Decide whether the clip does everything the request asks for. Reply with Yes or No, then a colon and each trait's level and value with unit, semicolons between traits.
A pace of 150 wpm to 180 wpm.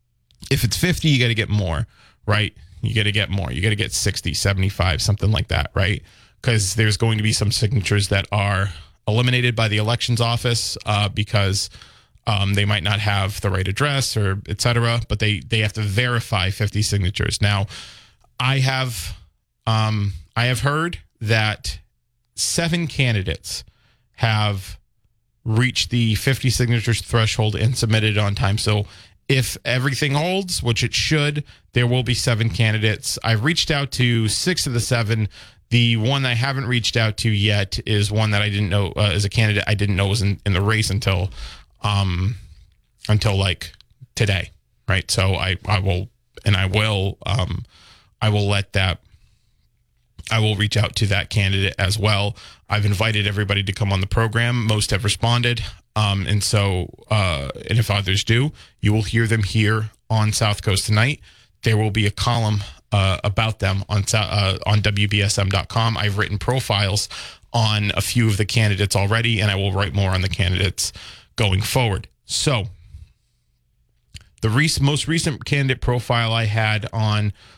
Yes: average, 170 wpm